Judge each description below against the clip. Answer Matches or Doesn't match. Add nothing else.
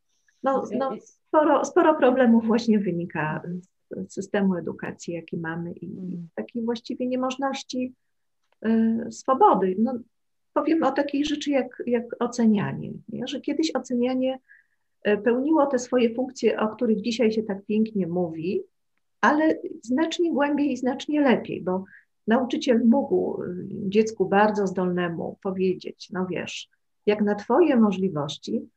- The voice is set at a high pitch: Matches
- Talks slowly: Doesn't match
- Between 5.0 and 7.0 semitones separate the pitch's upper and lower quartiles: Matches